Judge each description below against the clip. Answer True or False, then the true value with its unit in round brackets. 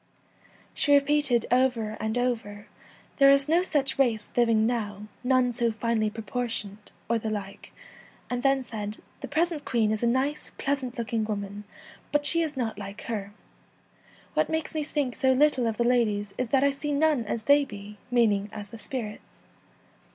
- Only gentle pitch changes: False (4.3 semitones)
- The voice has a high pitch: True (240 Hz)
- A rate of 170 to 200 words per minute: True (180 wpm)